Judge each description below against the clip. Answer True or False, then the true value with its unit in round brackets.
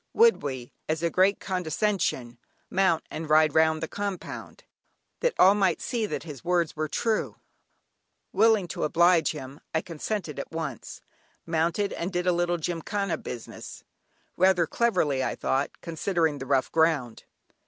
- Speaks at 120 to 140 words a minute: False (150 wpm)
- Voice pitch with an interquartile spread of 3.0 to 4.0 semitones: True (3.7 semitones)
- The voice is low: False (170 Hz)